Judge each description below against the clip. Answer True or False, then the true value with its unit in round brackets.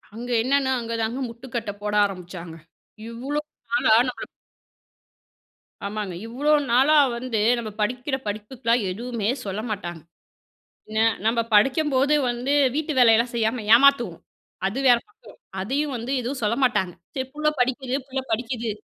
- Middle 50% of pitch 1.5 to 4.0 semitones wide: True (3.5 semitones)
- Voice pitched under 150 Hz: False (235 Hz)